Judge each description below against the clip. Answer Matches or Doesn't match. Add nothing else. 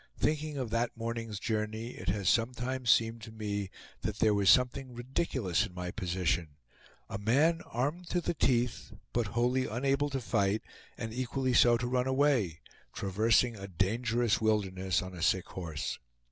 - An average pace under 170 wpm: Matches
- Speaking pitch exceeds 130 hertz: Doesn't match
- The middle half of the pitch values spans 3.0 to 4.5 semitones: Matches